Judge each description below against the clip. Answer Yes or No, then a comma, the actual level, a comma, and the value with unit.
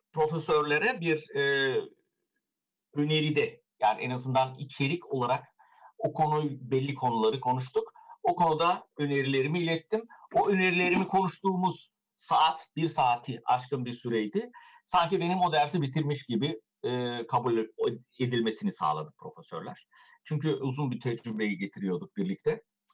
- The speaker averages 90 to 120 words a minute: Yes, average, 115 wpm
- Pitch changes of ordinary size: No, wide, 6.6 semitones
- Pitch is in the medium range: Yes, medium, 155 Hz